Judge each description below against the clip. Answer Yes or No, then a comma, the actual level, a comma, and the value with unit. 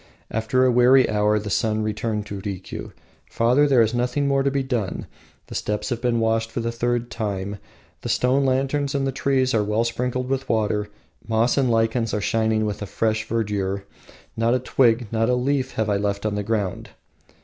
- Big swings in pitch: No, average, 3.1 semitones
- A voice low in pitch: Yes, low, 115 Hz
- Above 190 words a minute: Yes, average, 200 wpm